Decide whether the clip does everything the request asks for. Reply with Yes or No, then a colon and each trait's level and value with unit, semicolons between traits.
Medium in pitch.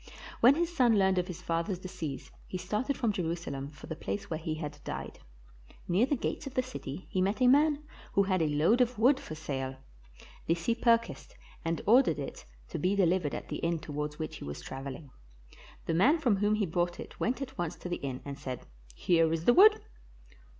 Yes: medium, 180 Hz